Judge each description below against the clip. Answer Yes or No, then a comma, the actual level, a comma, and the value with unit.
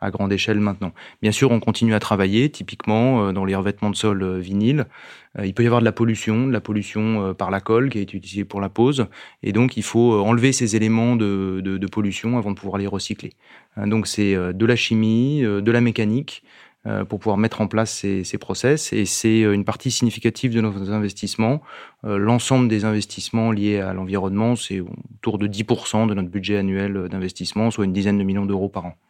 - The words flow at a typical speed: Yes, average, 205 wpm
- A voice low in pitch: Yes, low, 105 Hz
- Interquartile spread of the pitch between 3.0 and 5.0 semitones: No, narrow, 2.5 semitones